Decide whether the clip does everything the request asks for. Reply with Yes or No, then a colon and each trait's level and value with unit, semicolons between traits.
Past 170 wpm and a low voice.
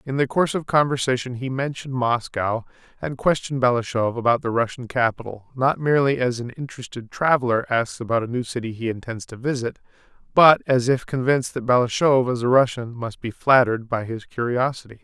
Yes: average, 180 wpm; low, 125 Hz